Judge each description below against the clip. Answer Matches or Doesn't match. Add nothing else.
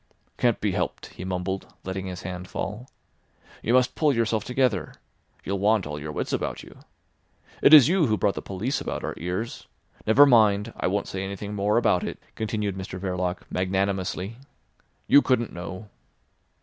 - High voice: Doesn't match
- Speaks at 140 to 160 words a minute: Doesn't match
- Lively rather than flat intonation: Doesn't match